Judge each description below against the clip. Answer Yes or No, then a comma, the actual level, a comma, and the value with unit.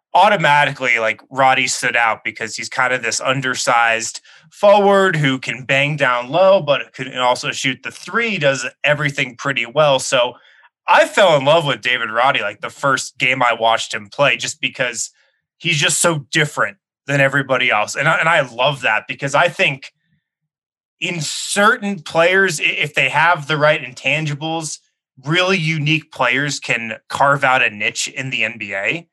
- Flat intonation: No, average, 3.9 semitones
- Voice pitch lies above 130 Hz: Yes, medium, 140 Hz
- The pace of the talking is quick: No, average, 165 wpm